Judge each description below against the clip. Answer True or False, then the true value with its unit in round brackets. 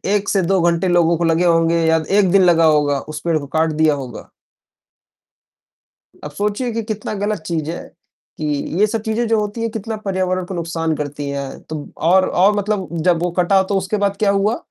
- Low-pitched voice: False (180 Hz)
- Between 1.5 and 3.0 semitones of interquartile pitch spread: False (4.1 semitones)